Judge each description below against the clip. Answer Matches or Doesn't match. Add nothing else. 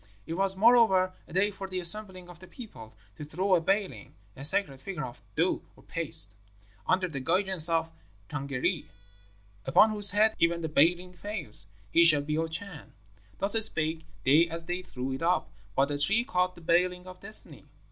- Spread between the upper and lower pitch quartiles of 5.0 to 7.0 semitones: Doesn't match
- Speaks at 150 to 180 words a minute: Doesn't match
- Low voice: Doesn't match